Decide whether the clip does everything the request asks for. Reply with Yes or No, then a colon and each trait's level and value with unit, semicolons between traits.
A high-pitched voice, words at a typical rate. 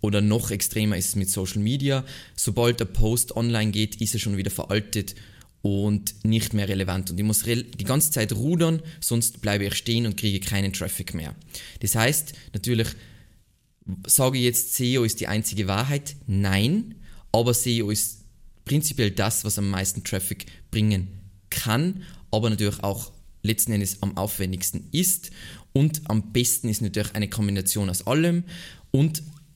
No: low, 110 Hz; average, 160 wpm